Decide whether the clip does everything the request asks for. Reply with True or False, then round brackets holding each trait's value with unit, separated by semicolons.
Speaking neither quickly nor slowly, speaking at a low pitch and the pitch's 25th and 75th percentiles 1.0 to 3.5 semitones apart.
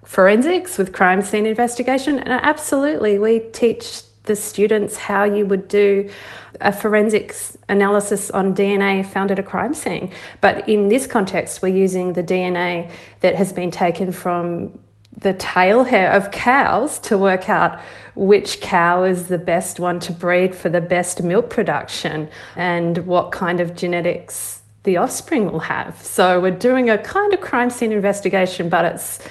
False (160 wpm; 195 Hz; 3.1 semitones)